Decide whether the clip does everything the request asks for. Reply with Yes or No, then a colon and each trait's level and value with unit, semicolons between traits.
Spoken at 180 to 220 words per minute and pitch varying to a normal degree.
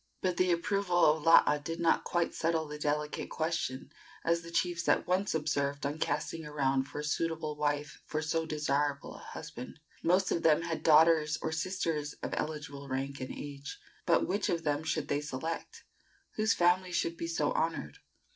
No: average, 185 wpm; narrow, 2.3 semitones